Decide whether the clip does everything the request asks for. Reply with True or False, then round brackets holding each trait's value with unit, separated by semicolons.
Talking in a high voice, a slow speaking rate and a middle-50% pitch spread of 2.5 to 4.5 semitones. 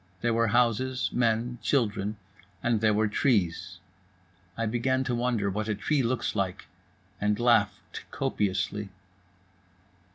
False (110 Hz; 125 wpm; 2.8 semitones)